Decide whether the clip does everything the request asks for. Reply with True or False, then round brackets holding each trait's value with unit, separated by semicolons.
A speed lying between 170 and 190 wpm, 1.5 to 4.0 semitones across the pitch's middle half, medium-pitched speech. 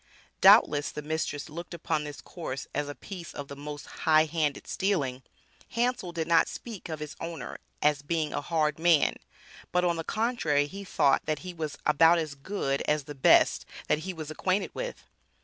True (185 wpm; 2.9 semitones; 155 Hz)